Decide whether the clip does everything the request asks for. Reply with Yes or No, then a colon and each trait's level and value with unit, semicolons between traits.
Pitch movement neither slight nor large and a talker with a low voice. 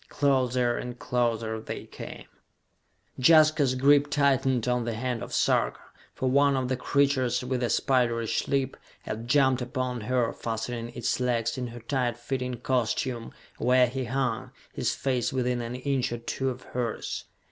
No: narrow, 1.8 semitones; low, 125 Hz